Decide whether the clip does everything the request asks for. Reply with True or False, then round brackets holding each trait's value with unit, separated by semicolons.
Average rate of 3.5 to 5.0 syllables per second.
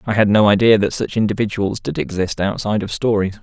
False (6.1 syllables/s)